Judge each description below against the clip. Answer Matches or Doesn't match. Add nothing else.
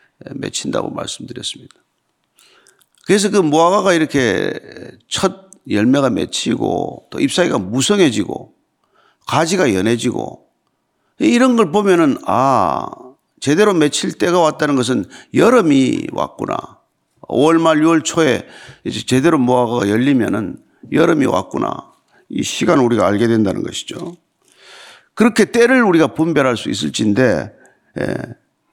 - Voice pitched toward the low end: Doesn't match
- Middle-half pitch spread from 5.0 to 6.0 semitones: Doesn't match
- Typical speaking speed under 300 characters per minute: Matches